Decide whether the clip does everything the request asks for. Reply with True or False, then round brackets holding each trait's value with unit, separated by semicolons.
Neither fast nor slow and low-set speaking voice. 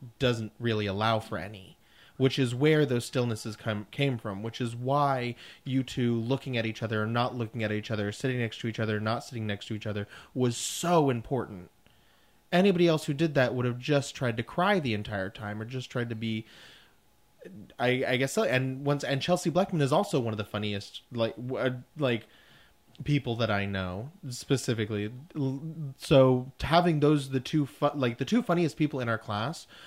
True (195 wpm; 125 Hz)